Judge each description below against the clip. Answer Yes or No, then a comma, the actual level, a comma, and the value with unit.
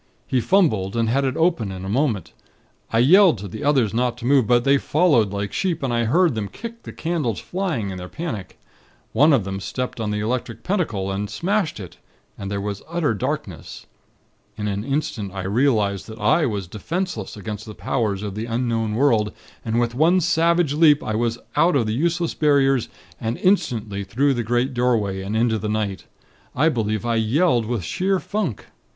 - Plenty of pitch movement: Yes, wide, 6.1 semitones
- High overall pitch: No, low, 120 Hz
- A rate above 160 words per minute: Yes, average, 195 wpm